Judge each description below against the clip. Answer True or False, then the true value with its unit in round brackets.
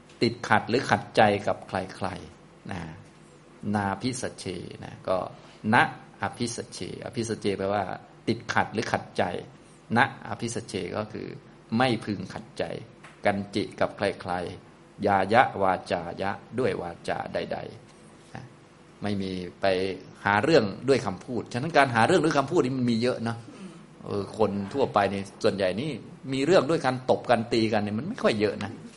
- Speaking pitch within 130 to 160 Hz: False (110 Hz)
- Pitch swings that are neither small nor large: True (4.2 semitones)